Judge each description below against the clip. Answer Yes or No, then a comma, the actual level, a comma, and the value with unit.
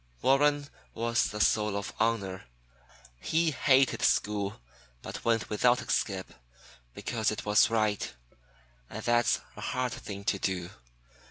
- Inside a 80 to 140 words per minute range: Yes, slow, 135 wpm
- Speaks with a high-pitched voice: No, low, 110 Hz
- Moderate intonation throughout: Yes, average, 3.2 semitones